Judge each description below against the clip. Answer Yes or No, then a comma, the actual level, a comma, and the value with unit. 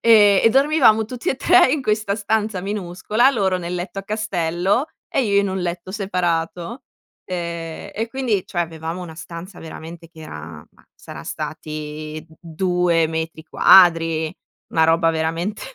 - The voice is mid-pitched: Yes, medium, 180 Hz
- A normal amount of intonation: Yes, average, 4.4 semitones